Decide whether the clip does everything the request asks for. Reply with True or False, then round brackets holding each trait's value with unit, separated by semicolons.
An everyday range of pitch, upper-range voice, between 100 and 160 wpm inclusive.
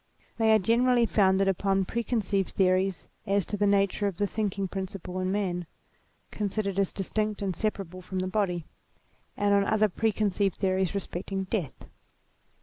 False (1.9 semitones; 195 Hz; 150 wpm)